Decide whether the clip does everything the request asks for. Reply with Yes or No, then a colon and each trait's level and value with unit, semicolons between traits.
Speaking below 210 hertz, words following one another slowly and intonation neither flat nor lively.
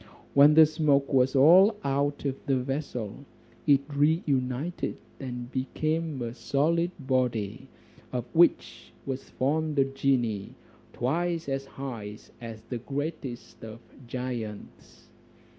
Yes: low, 135 Hz; slow, 120 wpm; average, 3.5 semitones